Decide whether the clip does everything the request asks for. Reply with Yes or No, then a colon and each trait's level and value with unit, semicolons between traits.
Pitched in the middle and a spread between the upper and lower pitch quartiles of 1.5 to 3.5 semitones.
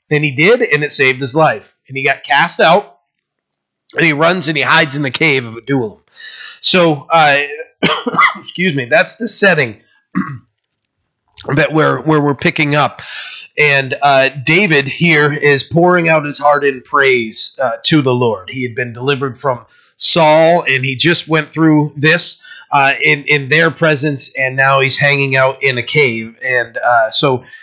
Yes: medium, 145 Hz; average, 3.0 semitones